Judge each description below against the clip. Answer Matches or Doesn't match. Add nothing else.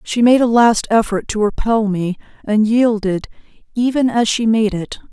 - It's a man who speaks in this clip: Doesn't match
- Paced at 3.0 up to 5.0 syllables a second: Matches